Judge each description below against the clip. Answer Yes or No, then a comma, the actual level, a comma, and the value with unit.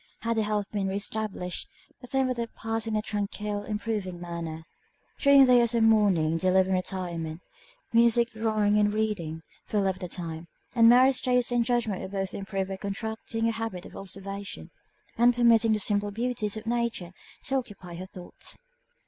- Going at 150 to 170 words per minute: No, average, 180 wpm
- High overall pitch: Yes, high, 210 Hz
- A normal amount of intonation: Yes, average, 3.3 semitones